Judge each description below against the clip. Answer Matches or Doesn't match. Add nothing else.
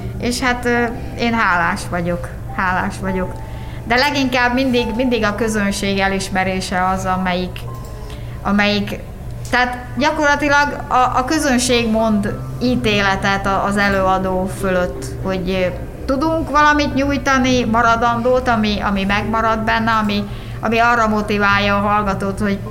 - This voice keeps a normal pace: Matches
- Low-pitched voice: Doesn't match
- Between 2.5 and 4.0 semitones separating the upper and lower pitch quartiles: Doesn't match